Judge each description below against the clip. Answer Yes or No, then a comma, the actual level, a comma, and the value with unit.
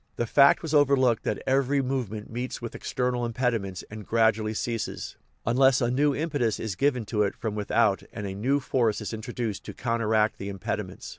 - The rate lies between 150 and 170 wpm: No, average, 190 wpm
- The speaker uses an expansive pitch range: No, average, 3.5 semitones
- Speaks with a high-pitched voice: No, low, 115 Hz